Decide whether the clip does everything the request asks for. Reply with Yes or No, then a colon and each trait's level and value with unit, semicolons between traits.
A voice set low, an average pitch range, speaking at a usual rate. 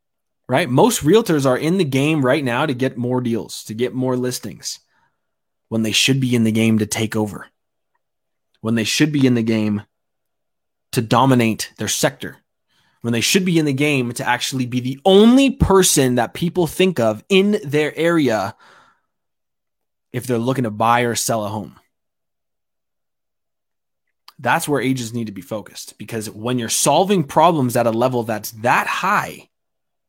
Yes: low, 125 Hz; average, 4.6 semitones; average, 170 wpm